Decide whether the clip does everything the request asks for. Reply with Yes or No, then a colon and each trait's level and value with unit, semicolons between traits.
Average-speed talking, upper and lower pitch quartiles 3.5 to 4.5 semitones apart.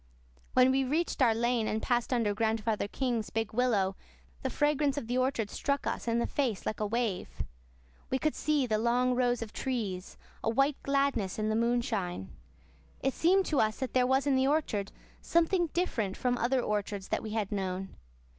Yes: average, 190 wpm; average, 3.8 semitones